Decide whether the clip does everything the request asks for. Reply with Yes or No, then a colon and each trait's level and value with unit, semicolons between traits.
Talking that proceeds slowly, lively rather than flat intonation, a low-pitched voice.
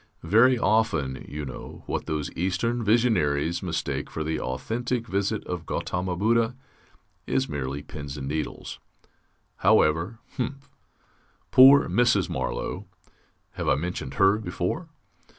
Yes: slow, 120 wpm; wide, 7.2 semitones; very low, 90 Hz